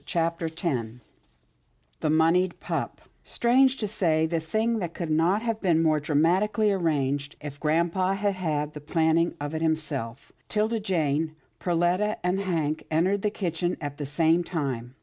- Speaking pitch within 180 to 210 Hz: No, medium, 165 Hz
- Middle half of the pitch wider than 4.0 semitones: No, average, 3.7 semitones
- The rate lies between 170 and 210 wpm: No, average, 150 wpm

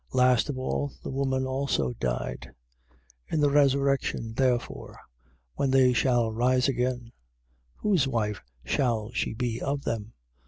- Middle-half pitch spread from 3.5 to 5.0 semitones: No, average, 3.0 semitones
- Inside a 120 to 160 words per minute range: Yes, average, 140 wpm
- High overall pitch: No, low, 130 Hz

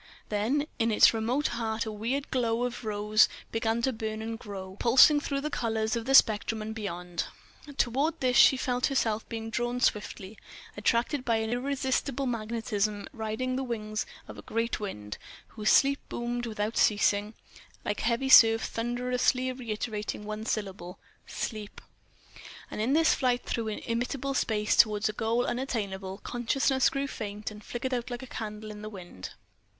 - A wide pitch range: No, average, 2.8 semitones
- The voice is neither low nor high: No, high, 225 Hz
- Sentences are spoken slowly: No, average, 165 wpm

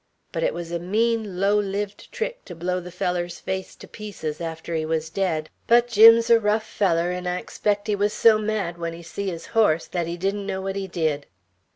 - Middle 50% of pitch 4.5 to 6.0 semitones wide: No, average, 3.5 semitones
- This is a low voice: No, high, 190 Hz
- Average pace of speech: No, fast, 220 wpm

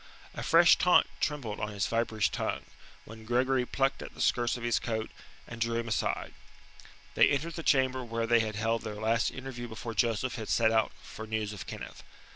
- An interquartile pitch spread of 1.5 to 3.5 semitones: Yes, narrow, 2.6 semitones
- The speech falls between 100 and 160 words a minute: No, average, 200 wpm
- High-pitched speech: No, low, 115 Hz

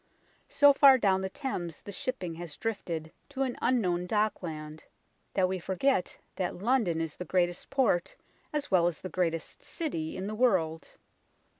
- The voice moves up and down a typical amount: No, wide, 6.2 semitones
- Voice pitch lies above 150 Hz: Yes, medium, 185 Hz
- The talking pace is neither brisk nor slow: Yes, average, 160 wpm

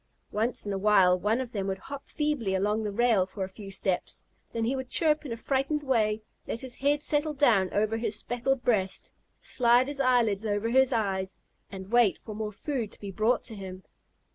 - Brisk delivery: Yes, fast, 210 wpm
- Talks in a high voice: Yes, high, 225 Hz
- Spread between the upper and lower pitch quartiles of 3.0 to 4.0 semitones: No, average, 4.5 semitones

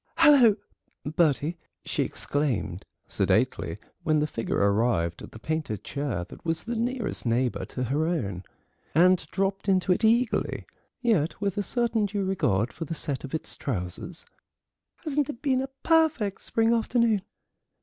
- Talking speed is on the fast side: No, average, 150 wpm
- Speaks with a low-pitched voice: No, medium, 175 Hz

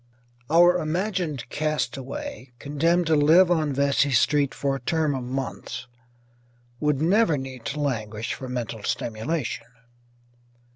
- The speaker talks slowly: Yes, slow, 125 wpm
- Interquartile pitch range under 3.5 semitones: No, average, 4.0 semitones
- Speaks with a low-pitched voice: No, medium, 145 Hz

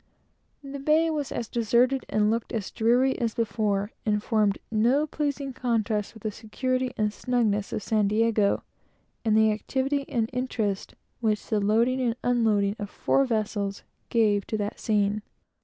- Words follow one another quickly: No, average, 155 wpm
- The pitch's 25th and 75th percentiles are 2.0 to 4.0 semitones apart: Yes, average, 3.2 semitones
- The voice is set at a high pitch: Yes, high, 225 Hz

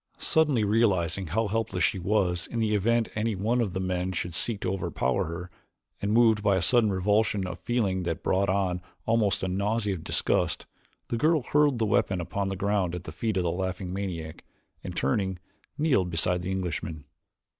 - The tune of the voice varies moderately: Yes, average, 3.6 semitones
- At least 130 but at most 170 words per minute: No, average, 190 wpm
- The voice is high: No, very low, 95 Hz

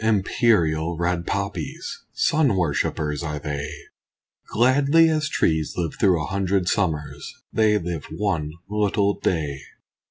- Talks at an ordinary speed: No, slow, 120 wpm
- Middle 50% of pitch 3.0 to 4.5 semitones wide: No, average, 5.1 semitones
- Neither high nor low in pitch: No, very low, 90 Hz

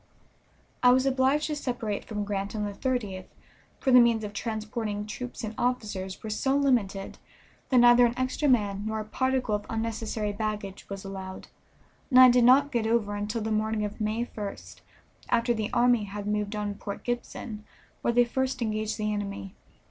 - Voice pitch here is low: No, high, 220 Hz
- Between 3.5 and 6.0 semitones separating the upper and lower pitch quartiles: No, average, 3.0 semitones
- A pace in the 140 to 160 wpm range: No, average, 180 wpm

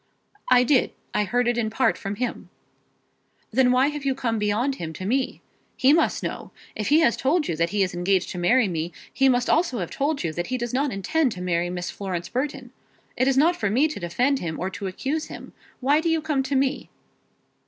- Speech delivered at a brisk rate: Yes, fast, 225 wpm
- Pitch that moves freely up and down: Yes, wide, 6.4 semitones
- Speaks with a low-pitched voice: No, high, 245 Hz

